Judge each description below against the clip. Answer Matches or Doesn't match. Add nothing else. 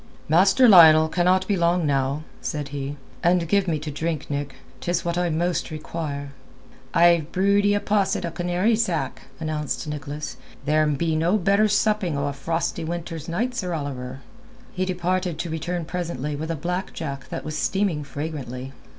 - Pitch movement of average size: Matches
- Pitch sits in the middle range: Matches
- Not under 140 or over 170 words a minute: Matches